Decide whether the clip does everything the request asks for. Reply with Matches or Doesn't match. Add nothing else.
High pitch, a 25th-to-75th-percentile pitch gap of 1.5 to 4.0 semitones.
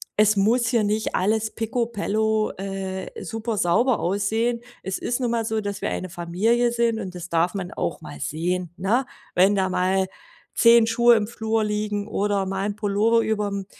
Matches